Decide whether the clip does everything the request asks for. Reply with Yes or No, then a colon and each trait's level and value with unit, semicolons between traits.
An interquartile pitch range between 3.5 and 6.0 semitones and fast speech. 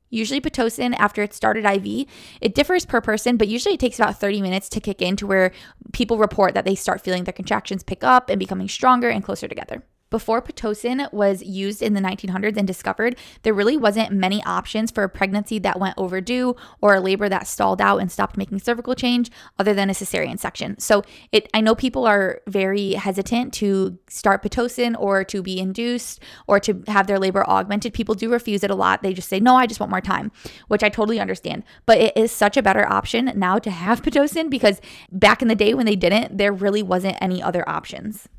No: average, 3.1 semitones; fast, 215 wpm